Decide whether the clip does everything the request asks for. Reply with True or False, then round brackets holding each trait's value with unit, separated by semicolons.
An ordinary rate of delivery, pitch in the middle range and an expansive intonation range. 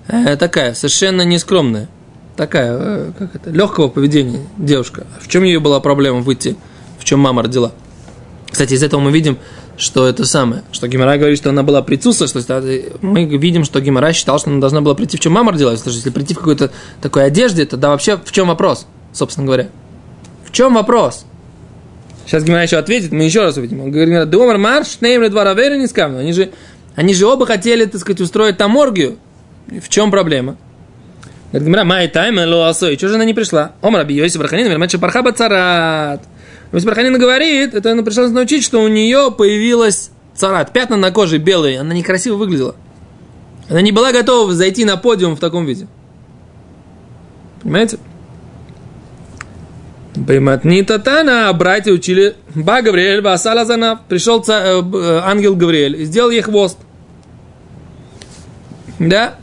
True (150 wpm; 180 Hz; 6.9 semitones)